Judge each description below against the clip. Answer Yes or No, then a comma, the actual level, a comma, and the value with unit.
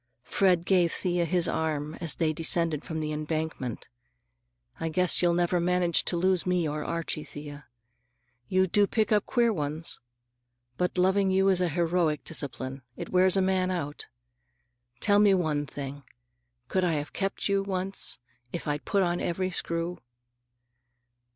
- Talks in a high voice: No, medium, 175 Hz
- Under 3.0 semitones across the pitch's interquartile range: No, average, 3.3 semitones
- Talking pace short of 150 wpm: No, average, 155 wpm